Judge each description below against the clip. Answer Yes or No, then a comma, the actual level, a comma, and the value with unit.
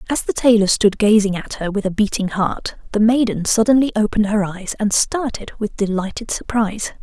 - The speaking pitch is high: Yes, high, 210 Hz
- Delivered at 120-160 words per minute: No, average, 190 wpm